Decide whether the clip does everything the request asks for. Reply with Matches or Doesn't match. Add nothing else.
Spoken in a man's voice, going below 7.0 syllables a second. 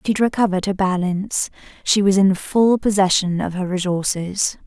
Doesn't match